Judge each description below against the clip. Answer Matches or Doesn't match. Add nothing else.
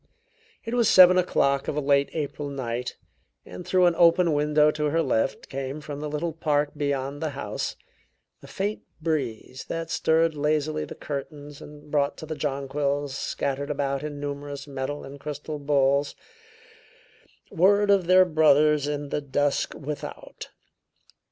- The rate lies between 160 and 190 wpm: Doesn't match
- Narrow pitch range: Matches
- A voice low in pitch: Doesn't match